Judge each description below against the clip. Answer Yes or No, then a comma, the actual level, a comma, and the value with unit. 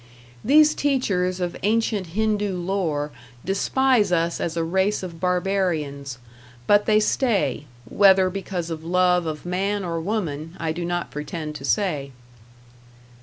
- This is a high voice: No, medium, 180 Hz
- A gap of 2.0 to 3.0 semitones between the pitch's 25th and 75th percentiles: No, average, 3.7 semitones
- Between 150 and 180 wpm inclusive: No, slow, 135 wpm